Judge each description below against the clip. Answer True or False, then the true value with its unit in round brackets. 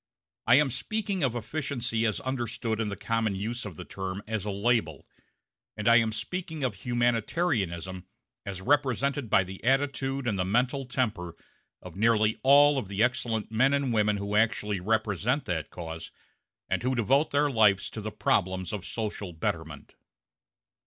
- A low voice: True (115 Hz)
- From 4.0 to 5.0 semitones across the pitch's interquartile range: True (4.6 semitones)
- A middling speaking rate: True (165 wpm)